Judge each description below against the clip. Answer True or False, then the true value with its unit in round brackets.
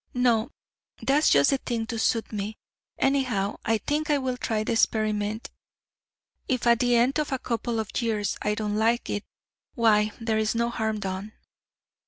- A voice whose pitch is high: True (225 Hz)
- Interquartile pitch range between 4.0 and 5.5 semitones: False (2.5 semitones)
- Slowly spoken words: False (175 wpm)